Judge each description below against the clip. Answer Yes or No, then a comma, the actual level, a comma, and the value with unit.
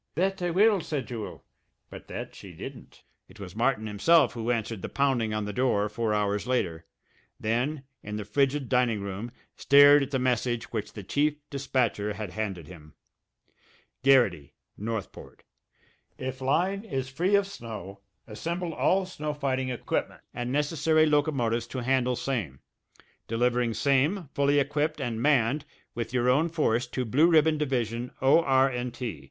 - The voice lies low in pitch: Yes, low, 125 Hz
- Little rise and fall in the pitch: No, average, 4.6 semitones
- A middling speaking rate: Yes, average, 155 wpm